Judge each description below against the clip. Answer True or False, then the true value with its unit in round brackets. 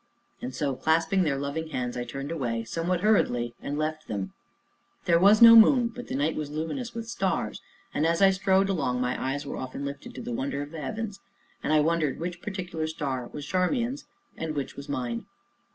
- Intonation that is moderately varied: False (5.9 semitones)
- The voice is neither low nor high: True (160 Hz)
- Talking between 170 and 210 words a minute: True (200 wpm)